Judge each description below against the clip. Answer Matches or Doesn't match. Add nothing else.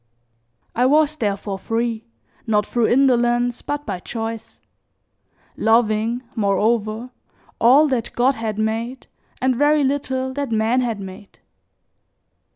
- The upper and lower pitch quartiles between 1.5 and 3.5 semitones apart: Matches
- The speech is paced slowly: Matches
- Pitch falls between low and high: Doesn't match